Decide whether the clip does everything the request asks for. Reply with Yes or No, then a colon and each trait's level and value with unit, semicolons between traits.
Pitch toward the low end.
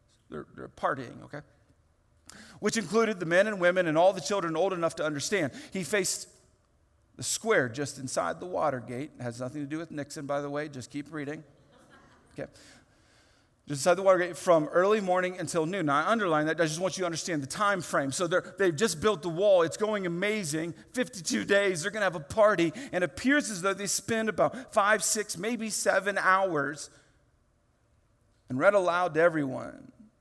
No: medium, 170 Hz